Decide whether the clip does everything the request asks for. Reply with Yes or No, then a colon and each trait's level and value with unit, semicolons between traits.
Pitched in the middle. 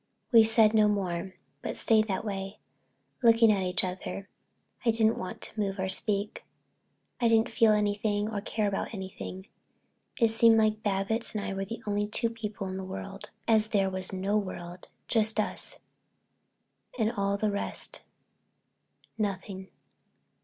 No: high, 205 Hz